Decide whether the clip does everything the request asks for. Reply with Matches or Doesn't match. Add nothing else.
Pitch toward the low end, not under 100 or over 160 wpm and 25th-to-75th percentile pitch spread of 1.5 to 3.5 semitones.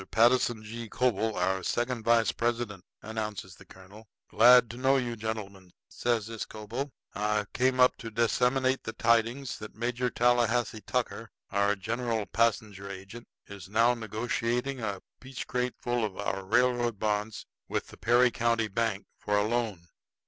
Matches